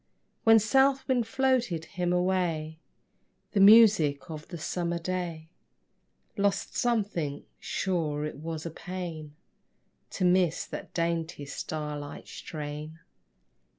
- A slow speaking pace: Yes, slow, 115 wpm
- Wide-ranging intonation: No, average, 4.0 semitones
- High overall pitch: No, medium, 170 Hz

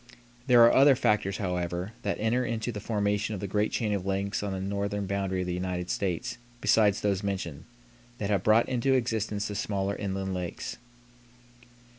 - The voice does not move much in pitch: Yes, narrow, 2.2 semitones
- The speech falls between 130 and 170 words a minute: No, average, 180 wpm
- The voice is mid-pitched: No, low, 100 Hz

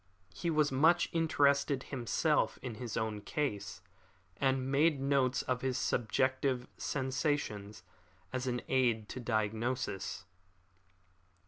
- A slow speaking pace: Yes, slow, 110 wpm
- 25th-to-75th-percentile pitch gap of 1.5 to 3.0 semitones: No, average, 3.7 semitones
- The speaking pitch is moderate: No, low, 130 Hz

